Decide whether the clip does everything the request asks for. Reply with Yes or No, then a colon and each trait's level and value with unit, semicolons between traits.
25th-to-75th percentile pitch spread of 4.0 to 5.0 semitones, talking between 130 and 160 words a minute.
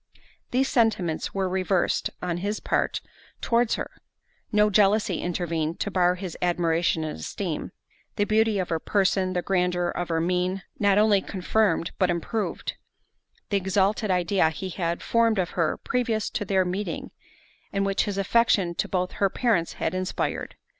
No: average, 2.8 semitones; average, 155 wpm